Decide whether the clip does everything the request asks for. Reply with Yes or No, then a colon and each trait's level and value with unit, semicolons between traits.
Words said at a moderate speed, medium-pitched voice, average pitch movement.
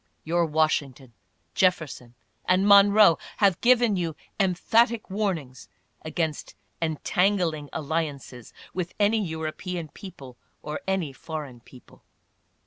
No: slow, 110 wpm; medium, 165 Hz; average, 4.6 semitones